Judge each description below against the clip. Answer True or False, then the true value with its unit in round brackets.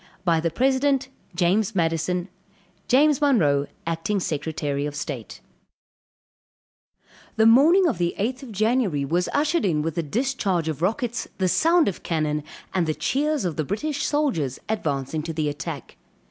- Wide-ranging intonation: True (8.8 semitones)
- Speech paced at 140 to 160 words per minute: True (150 wpm)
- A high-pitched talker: False (180 Hz)